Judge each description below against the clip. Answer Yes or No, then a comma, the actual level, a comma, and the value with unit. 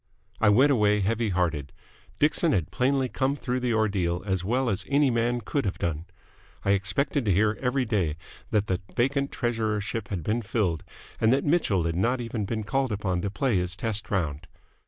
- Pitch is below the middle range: Yes, low, 110 Hz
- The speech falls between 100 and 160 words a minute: No, average, 190 wpm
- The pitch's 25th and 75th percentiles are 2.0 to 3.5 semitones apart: No, average, 4.9 semitones